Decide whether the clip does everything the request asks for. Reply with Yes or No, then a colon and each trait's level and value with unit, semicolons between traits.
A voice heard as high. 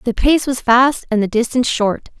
Yes: high, 245 Hz